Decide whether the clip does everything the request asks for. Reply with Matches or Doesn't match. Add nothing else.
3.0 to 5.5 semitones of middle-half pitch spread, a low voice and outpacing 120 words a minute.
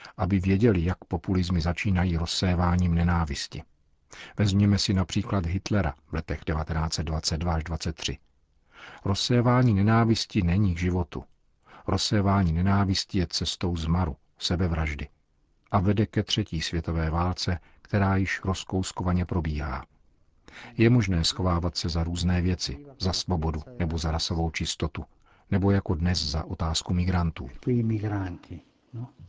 Doesn't match